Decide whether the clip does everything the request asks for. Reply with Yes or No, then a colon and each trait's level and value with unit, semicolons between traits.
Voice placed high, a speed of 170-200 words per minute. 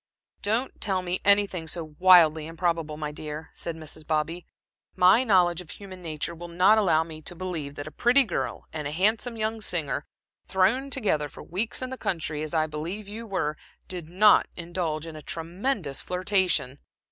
No: medium, 175 Hz; average, 180 wpm